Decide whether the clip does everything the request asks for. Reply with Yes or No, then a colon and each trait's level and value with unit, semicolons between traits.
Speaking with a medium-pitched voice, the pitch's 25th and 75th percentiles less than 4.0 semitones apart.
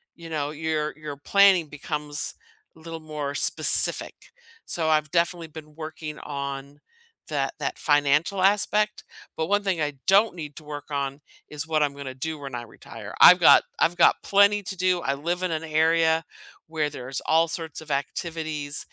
Yes: medium, 155 Hz; narrow, 2.4 semitones